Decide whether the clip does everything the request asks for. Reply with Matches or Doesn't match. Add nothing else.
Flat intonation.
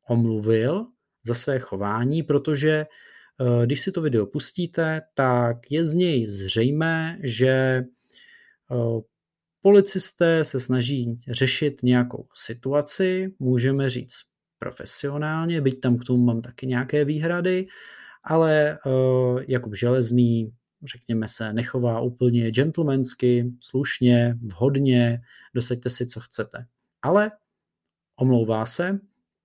Doesn't match